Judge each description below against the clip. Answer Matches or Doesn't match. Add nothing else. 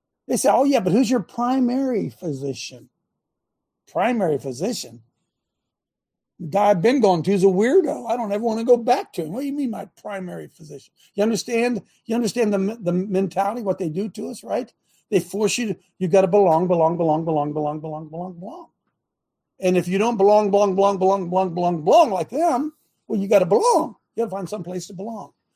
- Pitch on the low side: Doesn't match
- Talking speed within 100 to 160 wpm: Doesn't match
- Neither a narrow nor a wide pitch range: Matches